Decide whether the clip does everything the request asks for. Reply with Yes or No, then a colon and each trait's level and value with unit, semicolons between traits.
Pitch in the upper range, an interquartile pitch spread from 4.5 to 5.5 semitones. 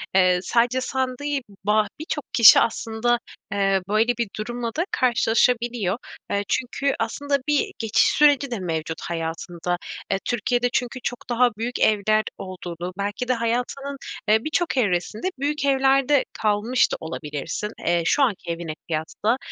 Yes: high, 230 Hz; average, 4.8 semitones